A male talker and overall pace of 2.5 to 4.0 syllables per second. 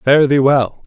Yes: male; 3.6 syllables/s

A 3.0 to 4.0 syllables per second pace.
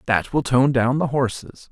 No: 4.5 syllables/s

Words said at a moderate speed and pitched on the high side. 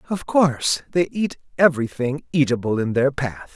No: average, 150 wpm; medium, 140 Hz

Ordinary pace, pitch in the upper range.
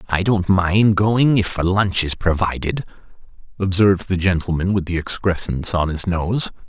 No: average, 160 wpm; very low, 95 Hz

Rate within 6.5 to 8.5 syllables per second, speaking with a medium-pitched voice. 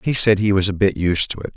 No: 6.6 syllables/s; low, 100 Hz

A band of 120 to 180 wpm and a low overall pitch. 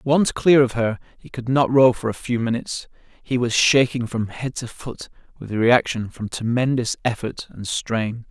No: average, 195 wpm; low, 120 Hz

